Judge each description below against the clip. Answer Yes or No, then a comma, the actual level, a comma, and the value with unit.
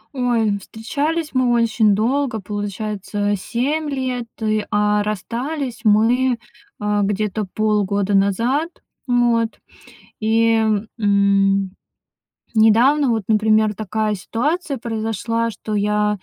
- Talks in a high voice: Yes, high, 220 Hz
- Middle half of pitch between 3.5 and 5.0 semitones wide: No, average, 2.8 semitones